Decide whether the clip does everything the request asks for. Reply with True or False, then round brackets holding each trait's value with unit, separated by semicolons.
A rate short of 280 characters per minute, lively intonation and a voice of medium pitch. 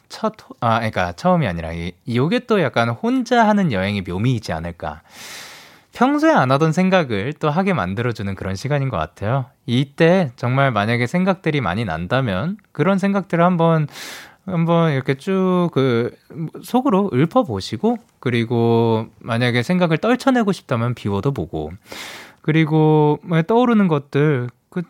False (310 characters per minute; 7.7 semitones; 145 Hz)